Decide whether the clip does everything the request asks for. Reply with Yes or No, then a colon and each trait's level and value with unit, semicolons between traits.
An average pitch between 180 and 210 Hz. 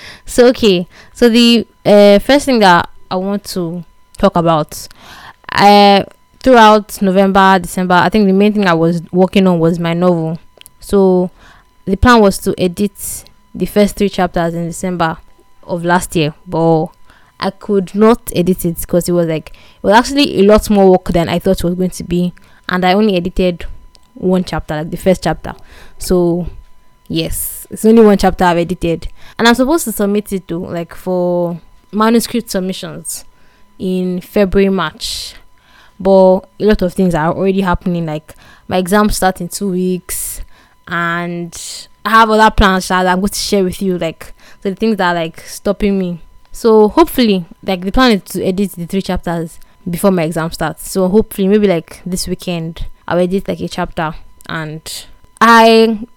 Yes: medium, 185 Hz